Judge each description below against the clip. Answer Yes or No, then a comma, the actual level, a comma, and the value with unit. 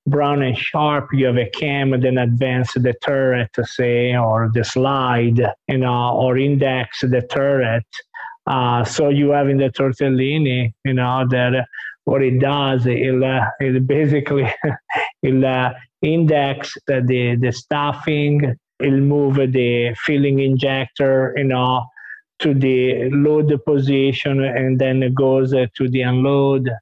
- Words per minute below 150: Yes, average, 140 wpm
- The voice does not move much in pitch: Yes, narrow, 1.9 semitones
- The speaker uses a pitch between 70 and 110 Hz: No, low, 130 Hz